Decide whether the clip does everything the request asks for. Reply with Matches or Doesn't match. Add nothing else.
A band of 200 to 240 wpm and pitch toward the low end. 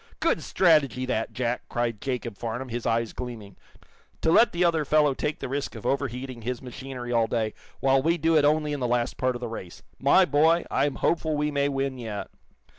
Matches